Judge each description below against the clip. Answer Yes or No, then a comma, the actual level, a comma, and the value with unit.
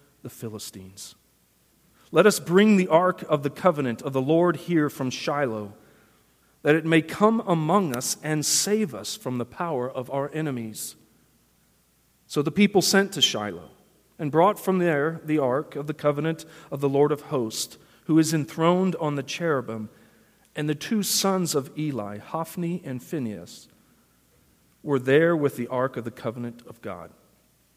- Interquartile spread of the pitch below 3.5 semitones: No, average, 5.0 semitones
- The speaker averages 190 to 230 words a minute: No, average, 165 wpm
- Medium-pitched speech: Yes, medium, 150 Hz